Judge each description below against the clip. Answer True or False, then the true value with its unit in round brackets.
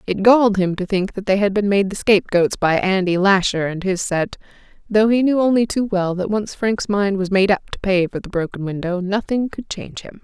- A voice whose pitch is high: True (195 Hz)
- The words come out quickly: True (235 wpm)